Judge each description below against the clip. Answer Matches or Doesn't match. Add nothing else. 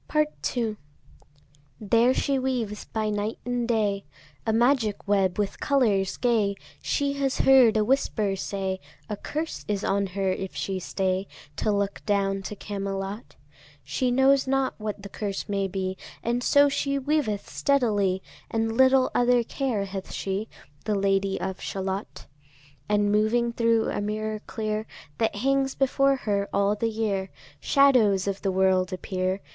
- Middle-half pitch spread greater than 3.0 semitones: Matches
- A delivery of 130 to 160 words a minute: Matches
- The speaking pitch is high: Matches